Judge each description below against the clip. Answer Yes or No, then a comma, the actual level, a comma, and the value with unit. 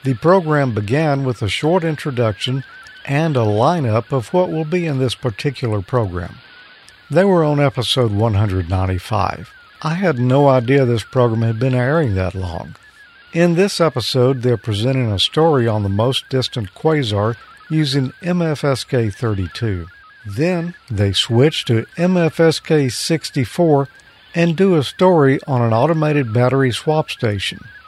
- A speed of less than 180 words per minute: Yes, average, 140 wpm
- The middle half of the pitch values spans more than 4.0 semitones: Yes, wide, 5.5 semitones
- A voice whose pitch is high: No, low, 135 Hz